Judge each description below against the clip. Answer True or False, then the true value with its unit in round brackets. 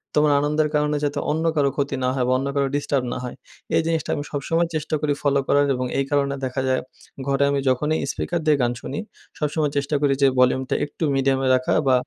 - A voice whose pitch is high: False (140 Hz)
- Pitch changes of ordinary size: False (1.8 semitones)